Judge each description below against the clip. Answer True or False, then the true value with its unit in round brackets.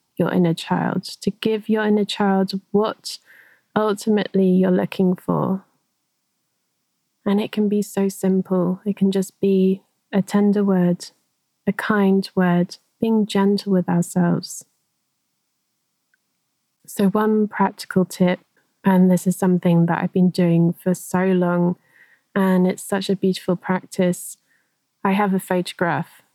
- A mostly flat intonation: True (1.9 semitones)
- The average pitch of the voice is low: False (190 Hz)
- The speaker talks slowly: True (130 wpm)